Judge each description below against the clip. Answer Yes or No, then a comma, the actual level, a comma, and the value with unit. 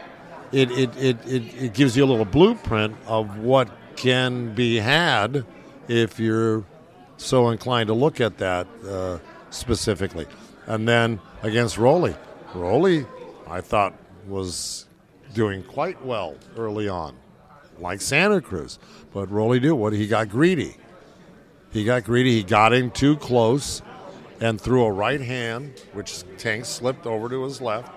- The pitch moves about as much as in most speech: Yes, average, 3.4 semitones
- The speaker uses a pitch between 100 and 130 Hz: Yes, low, 115 Hz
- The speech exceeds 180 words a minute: No, average, 145 wpm